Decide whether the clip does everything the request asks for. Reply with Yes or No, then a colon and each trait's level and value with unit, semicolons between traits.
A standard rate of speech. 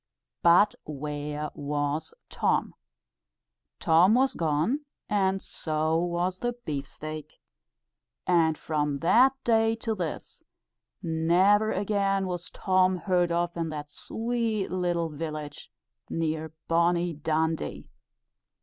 No: slow, 105 wpm